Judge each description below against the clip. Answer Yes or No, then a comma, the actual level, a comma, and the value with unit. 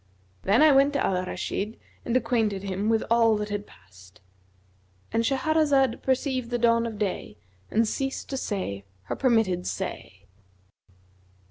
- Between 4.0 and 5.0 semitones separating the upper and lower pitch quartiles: Yes, average, 4.4 semitones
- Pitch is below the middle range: No, high, 225 Hz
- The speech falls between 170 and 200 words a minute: No, average, 145 wpm